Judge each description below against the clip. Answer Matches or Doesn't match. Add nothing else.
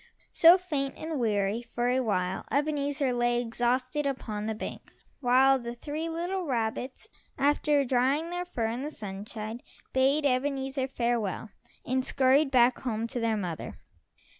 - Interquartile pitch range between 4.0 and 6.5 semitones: Doesn't match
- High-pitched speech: Matches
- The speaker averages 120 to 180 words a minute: Matches